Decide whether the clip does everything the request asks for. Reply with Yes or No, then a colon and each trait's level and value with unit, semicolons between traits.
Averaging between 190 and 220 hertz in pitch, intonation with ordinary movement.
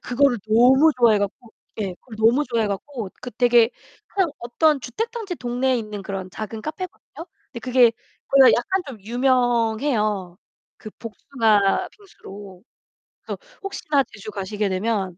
No: high, 235 Hz; average, 4.2 semitones